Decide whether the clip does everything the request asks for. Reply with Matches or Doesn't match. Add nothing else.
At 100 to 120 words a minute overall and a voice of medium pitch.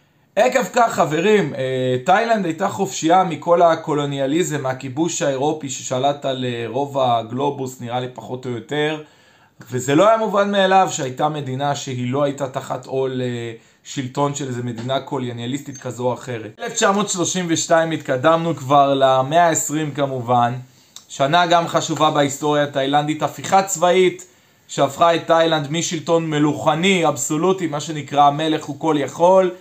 Doesn't match